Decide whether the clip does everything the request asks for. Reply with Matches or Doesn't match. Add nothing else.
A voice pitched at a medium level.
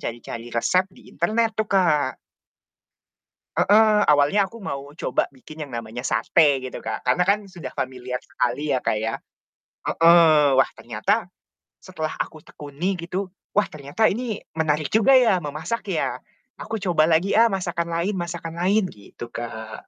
Matches